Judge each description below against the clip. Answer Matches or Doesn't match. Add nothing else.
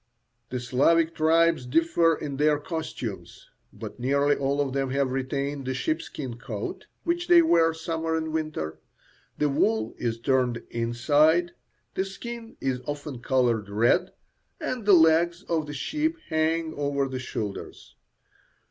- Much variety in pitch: Doesn't match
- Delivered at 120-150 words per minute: Matches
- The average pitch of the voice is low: Doesn't match